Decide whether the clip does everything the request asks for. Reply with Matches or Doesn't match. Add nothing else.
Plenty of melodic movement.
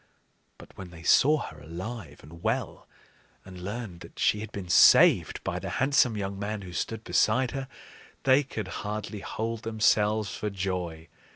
Doesn't match